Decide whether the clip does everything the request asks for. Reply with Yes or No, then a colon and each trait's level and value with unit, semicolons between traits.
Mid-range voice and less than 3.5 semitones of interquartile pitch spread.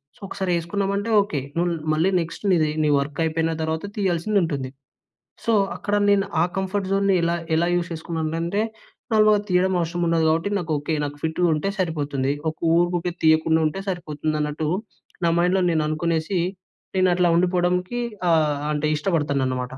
Yes: medium, 170 Hz; average, 3.0 semitones